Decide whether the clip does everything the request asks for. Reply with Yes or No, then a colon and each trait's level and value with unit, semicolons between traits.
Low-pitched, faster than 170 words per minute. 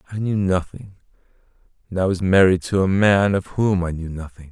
Yes: very low, 95 Hz; average, 200 wpm